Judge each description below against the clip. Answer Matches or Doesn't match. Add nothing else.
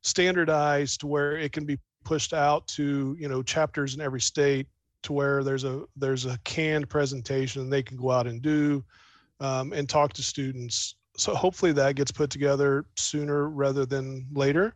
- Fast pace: Doesn't match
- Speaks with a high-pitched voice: Doesn't match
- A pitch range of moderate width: Doesn't match